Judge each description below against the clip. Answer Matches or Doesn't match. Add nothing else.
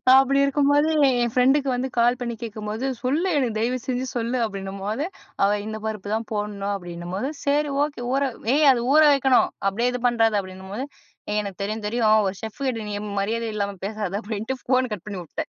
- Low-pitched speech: Doesn't match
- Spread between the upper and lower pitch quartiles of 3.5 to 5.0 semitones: Matches